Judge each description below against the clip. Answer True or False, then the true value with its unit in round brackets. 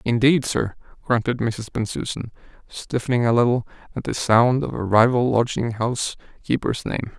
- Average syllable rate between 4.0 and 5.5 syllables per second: True (5.0 syllables/s)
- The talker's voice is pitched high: False (120 Hz)